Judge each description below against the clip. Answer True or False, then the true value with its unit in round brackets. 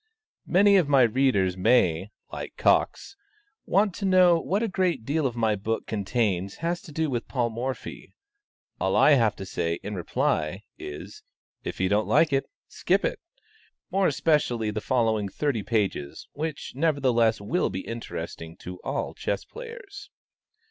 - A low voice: True (125 Hz)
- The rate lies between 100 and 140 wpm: False (155 wpm)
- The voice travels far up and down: True (8.0 semitones)